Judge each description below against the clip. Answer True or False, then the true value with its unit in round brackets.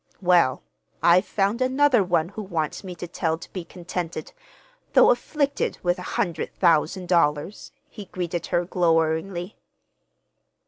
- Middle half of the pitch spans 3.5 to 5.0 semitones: False (2.8 semitones)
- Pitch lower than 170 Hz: False (180 Hz)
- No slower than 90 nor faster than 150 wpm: True (140 wpm)